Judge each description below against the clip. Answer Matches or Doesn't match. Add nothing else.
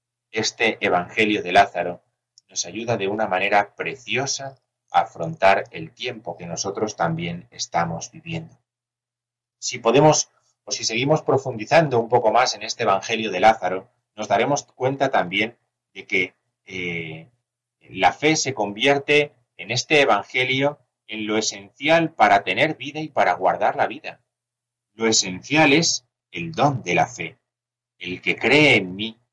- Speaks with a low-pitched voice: Matches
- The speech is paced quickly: Doesn't match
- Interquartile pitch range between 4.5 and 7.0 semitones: Matches